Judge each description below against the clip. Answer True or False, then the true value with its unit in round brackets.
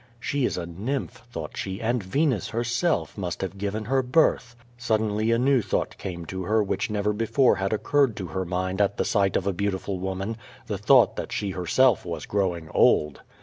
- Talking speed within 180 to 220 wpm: True (190 wpm)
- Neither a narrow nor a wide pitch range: True (4.1 semitones)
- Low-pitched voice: True (100 Hz)